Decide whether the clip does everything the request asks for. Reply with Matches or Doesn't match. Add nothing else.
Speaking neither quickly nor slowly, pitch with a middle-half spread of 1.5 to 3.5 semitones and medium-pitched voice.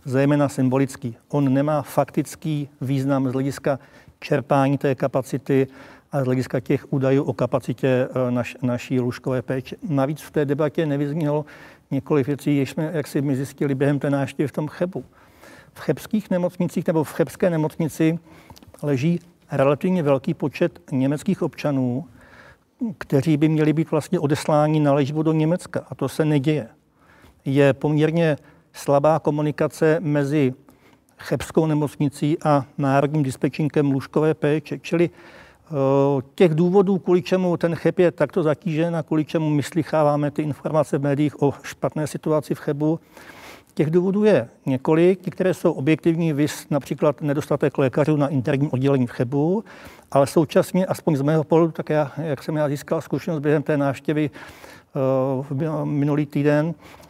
Matches